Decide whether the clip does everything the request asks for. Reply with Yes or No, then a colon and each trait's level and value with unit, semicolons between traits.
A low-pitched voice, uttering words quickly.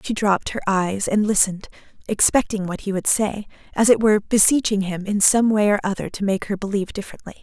No: high, 205 Hz; fast, 210 wpm